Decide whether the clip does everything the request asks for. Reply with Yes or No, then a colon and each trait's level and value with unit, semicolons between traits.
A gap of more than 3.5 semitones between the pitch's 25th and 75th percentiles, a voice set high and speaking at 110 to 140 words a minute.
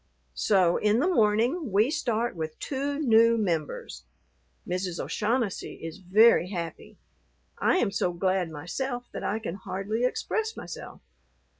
Yes: average, 5.1 semitones; high, 210 Hz; slow, 135 wpm